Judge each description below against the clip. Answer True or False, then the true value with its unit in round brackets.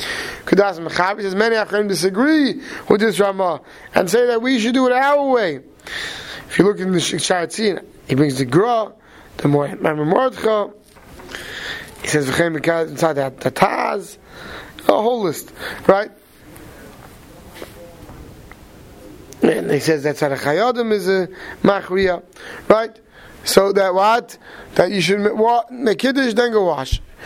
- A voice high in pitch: True (200 Hz)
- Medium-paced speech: True (150 wpm)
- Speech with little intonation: False (5.1 semitones)